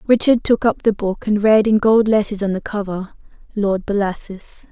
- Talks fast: No, average, 190 wpm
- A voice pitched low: No, high, 205 Hz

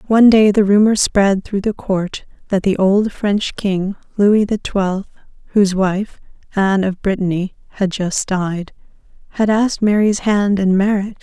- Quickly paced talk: No, average, 160 wpm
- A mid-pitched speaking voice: No, high, 200 Hz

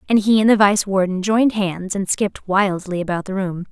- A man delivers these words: No, female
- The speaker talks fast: Yes, fast, 225 wpm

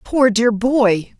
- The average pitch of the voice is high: Yes, high, 230 Hz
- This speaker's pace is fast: No, average, 150 wpm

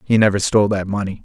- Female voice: No, male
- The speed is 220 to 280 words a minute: Yes, fast, 240 wpm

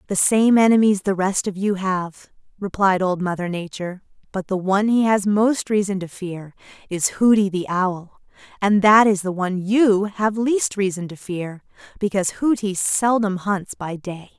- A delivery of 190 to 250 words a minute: No, average, 175 wpm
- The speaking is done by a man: No, female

